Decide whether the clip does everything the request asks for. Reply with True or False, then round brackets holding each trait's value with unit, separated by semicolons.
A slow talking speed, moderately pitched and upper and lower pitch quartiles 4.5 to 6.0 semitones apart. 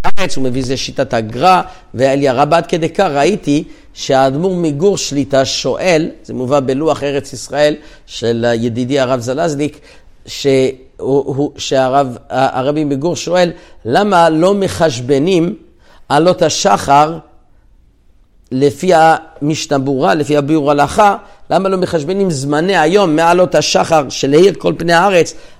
False (115 wpm; 145 Hz; 4.0 semitones)